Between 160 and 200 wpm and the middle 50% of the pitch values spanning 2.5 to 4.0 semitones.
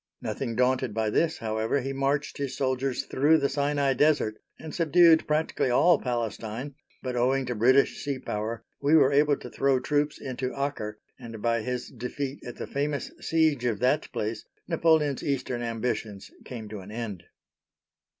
Yes: average, 165 wpm; average, 3.6 semitones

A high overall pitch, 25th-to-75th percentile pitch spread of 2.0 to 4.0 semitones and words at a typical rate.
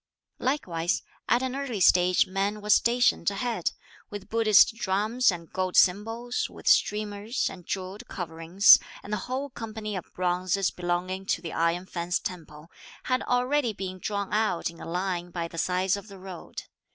Yes: high, 195 Hz; average, 3.6 semitones; average, 165 wpm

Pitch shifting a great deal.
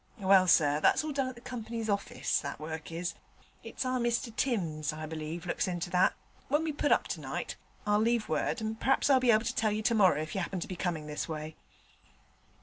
Yes: wide, 6.5 semitones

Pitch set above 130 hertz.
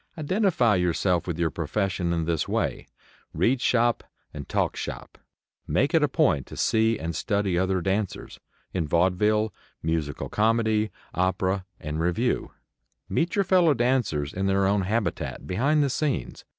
No: low, 100 Hz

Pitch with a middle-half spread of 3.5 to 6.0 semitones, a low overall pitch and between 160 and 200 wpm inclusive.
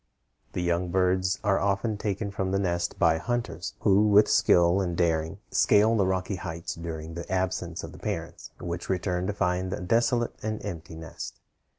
No: average, 2.7 semitones; very low, 95 Hz; average, 180 wpm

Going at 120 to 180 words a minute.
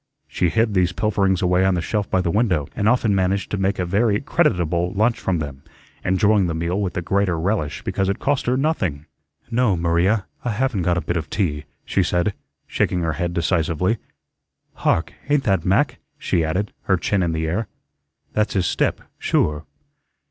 No: average, 190 wpm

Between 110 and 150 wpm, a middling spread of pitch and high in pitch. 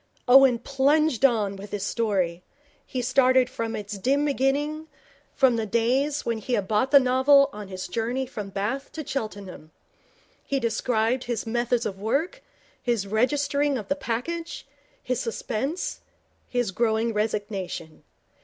Yes: average, 145 wpm; average, 4.3 semitones; high, 240 Hz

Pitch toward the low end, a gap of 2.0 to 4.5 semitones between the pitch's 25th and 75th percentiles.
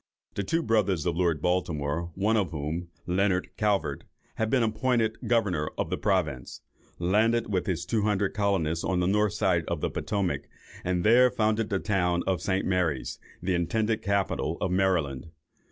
Yes: very low, 95 Hz; average, 3.6 semitones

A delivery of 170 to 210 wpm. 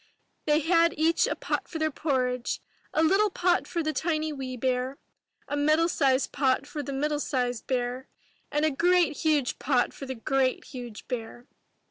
Yes: average, 180 wpm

